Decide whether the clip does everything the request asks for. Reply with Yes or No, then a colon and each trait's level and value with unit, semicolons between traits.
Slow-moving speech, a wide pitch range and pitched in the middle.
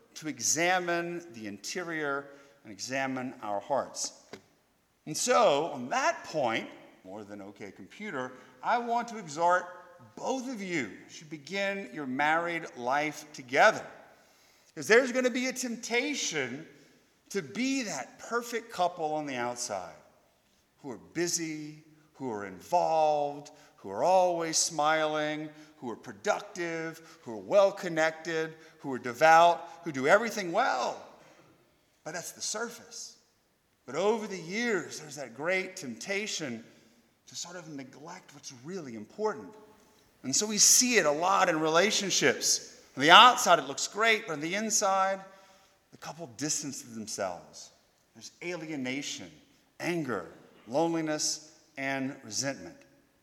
Yes: slow, 130 wpm; wide, 5.9 semitones; medium, 160 Hz